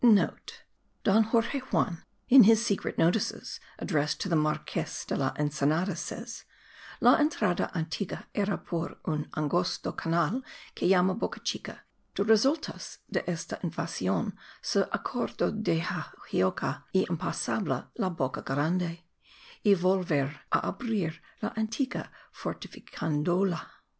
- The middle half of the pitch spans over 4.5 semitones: Yes, wide, 5.4 semitones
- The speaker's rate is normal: No, slow, 125 wpm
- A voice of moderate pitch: Yes, medium, 180 Hz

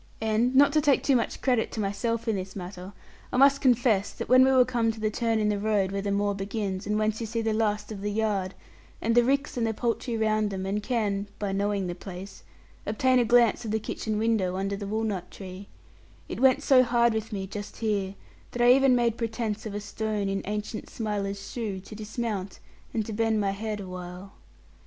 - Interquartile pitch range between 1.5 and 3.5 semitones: Yes, narrow, 2.6 semitones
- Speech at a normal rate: No, fast, 220 wpm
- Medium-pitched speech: No, high, 215 Hz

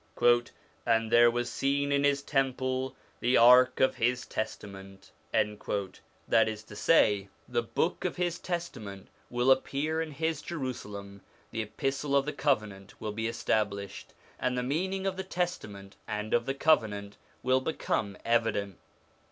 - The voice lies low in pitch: Yes, low, 120 Hz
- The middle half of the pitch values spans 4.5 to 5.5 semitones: Yes, average, 5.1 semitones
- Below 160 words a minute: Yes, average, 150 wpm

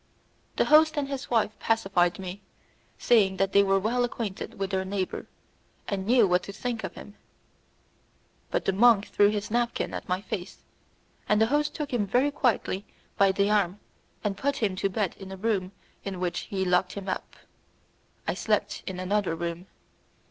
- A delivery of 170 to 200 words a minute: Yes, average, 180 wpm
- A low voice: No, high, 200 Hz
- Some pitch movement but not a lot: Yes, average, 3.3 semitones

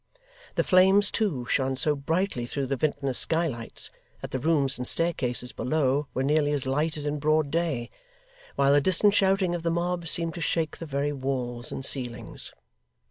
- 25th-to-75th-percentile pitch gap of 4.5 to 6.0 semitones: No, average, 4.0 semitones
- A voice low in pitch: No, medium, 145 Hz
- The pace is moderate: Yes, average, 180 wpm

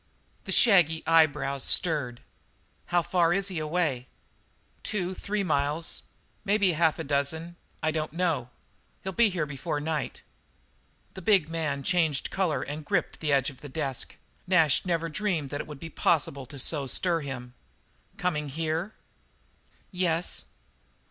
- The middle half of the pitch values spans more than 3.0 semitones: Yes, average, 3.7 semitones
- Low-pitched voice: No, medium, 160 Hz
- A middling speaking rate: Yes, average, 150 wpm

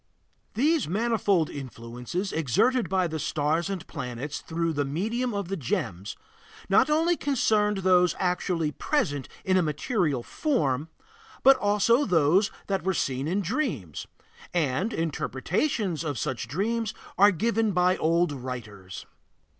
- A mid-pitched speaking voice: Yes, medium, 180 Hz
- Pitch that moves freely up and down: Yes, wide, 6.4 semitones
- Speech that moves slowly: Yes, slow, 130 wpm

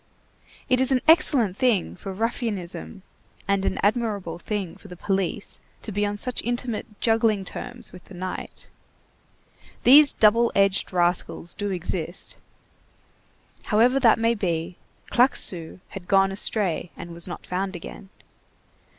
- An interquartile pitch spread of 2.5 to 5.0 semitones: Yes, average, 4.1 semitones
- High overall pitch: Yes, high, 200 Hz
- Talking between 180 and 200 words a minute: No, slow, 135 wpm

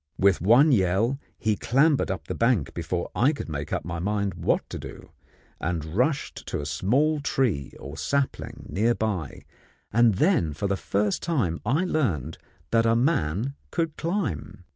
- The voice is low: Yes, low, 105 Hz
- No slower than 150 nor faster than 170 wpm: Yes, average, 165 wpm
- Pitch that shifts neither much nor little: No, wide, 7.9 semitones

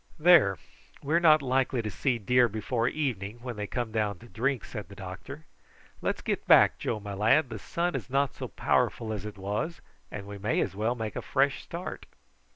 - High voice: No, low, 120 Hz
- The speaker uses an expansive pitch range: No, average, 4.7 semitones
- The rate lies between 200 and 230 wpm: Yes, fast, 205 wpm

